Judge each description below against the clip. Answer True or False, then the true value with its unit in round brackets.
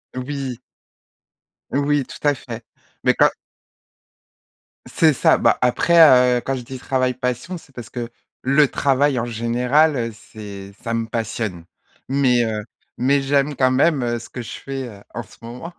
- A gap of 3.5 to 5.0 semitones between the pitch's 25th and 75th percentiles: False (2.9 semitones)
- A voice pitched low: True (125 Hz)